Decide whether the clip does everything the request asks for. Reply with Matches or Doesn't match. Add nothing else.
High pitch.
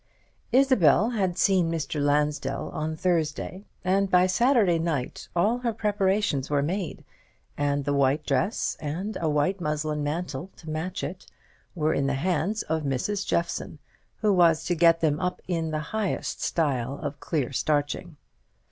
Doesn't match